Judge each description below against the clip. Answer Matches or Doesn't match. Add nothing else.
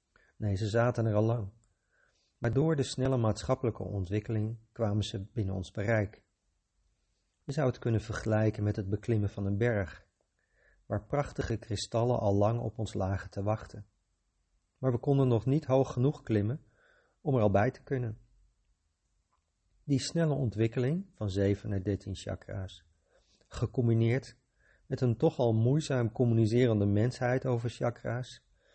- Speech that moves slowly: Doesn't match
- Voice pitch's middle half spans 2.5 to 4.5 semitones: Matches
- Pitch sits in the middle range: Doesn't match